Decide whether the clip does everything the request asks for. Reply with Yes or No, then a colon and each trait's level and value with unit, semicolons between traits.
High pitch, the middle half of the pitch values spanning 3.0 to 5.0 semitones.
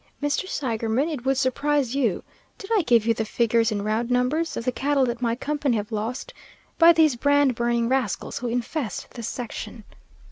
Yes: high, 245 Hz; average, 3.7 semitones